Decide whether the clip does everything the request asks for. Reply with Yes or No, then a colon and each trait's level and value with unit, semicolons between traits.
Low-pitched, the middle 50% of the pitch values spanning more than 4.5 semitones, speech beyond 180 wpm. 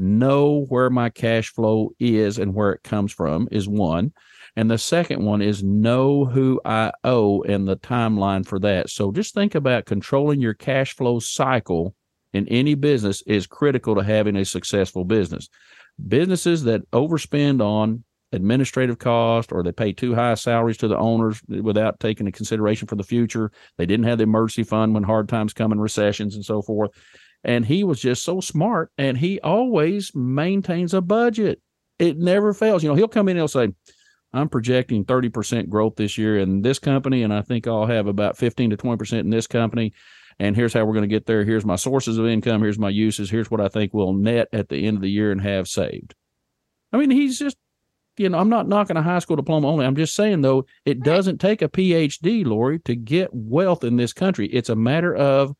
Yes: low, 115 Hz; average, 5.3 semitones; fast, 205 wpm